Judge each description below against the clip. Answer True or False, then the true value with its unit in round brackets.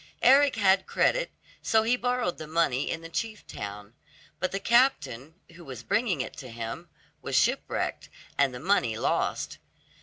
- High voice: False (170 Hz)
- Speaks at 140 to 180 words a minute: True (160 wpm)